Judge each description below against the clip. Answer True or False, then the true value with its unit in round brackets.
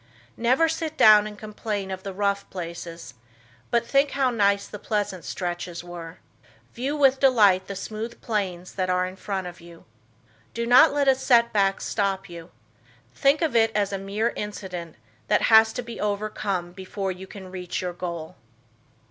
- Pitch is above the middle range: True (200 Hz)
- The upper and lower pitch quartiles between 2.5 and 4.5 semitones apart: True (4.1 semitones)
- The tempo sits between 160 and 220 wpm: True (170 wpm)